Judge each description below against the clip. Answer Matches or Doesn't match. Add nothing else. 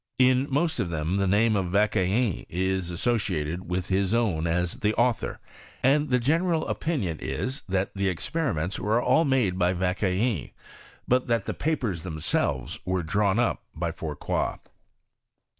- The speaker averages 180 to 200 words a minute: Doesn't match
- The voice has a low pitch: Matches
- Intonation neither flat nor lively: Doesn't match